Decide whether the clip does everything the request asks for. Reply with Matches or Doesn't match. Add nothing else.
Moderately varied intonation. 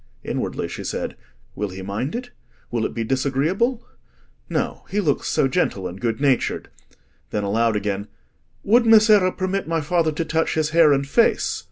Doesn't match